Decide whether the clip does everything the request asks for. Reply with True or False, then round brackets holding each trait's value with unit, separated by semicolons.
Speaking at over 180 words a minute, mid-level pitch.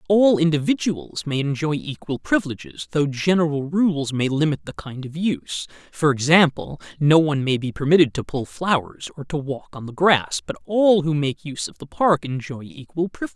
True (190 wpm; 150 Hz)